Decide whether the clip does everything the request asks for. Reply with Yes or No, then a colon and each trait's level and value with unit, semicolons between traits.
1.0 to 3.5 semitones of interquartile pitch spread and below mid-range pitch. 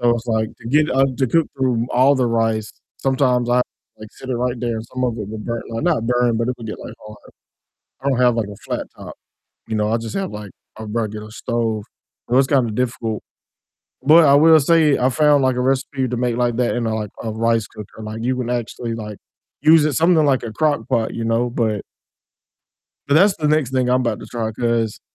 Yes: average, 2.9 semitones; low, 120 Hz